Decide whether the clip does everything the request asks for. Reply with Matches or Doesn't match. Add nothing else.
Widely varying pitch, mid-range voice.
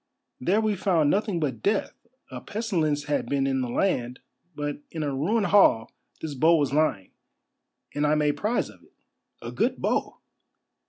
Matches